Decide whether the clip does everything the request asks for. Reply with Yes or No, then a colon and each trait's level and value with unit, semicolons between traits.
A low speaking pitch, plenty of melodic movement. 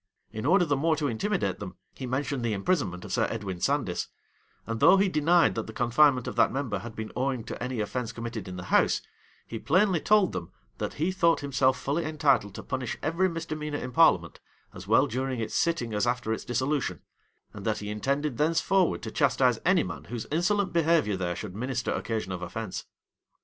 Yes: low, 130 Hz; wide, 6.1 semitones